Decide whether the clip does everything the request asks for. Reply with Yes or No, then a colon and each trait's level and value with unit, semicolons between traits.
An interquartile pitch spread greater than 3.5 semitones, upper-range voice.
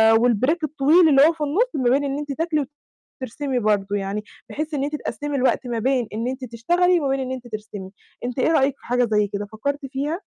Yes: average, 4.2 semitones; very high, 265 Hz